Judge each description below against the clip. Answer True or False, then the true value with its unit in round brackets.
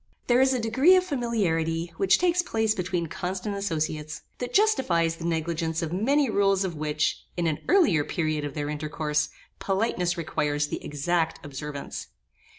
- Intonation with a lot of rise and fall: True (6.2 semitones)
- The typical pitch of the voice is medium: True (170 Hz)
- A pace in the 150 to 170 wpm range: True (155 wpm)